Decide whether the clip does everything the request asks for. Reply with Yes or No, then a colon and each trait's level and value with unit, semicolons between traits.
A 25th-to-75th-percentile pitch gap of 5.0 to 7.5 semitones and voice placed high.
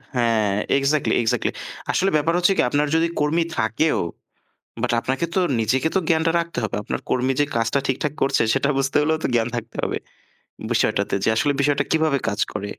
No: average, 5.3 semitones; medium, 140 Hz